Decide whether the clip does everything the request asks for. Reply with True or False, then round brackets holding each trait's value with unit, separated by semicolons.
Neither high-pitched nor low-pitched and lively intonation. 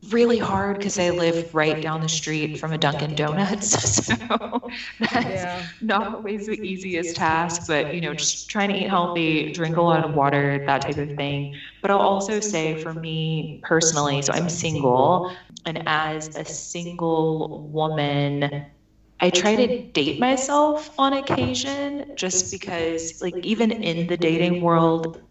False (165 Hz; 4.4 semitones)